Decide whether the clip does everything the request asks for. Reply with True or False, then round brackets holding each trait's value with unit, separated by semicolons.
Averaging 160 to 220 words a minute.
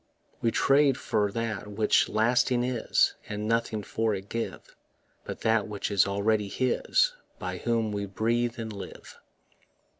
False (145 wpm)